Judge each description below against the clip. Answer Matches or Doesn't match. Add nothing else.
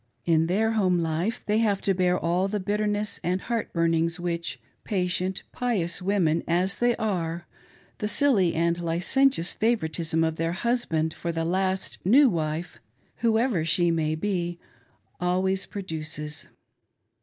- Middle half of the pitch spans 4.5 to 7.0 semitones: Doesn't match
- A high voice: Doesn't match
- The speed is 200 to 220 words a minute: Doesn't match